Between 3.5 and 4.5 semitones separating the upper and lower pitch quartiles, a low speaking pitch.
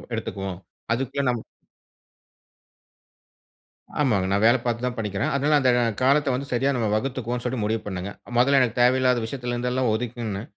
No: average, 2.8 semitones; low, 125 Hz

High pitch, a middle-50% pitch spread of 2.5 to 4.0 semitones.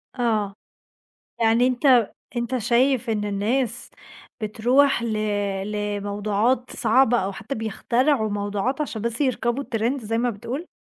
Yes: high, 235 Hz; average, 3.2 semitones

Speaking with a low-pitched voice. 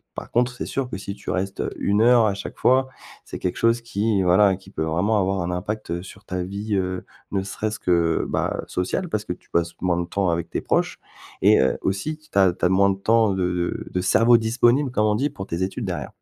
Yes: low, 100 Hz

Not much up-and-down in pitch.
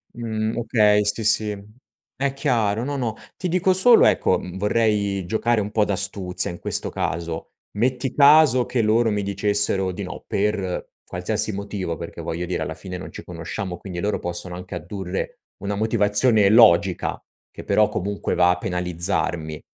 No: average, 3.6 semitones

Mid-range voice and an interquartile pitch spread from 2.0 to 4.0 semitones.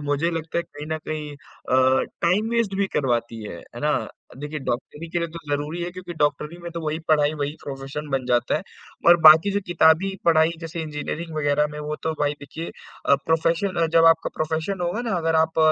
Yes: medium, 155 Hz; narrow, 2.5 semitones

